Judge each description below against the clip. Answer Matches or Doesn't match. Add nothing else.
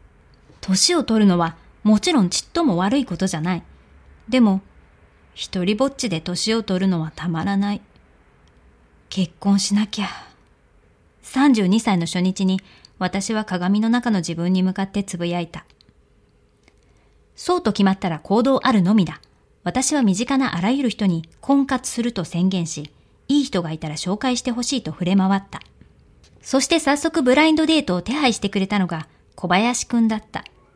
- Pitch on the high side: Matches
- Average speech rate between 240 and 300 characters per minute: Matches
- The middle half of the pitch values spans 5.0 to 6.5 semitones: Matches